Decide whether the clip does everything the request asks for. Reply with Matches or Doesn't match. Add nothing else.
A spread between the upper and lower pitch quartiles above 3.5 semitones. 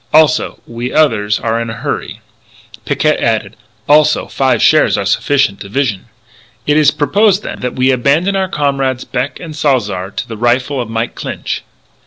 Matches